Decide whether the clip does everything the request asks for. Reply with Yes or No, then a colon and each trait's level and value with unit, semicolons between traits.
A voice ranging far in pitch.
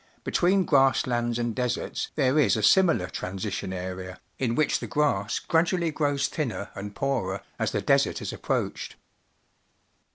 Yes: wide, 6.9 semitones